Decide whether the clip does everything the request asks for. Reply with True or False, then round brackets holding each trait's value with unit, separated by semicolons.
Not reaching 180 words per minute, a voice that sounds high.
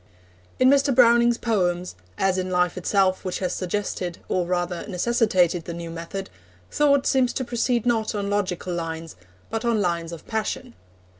True (160 wpm; 195 Hz)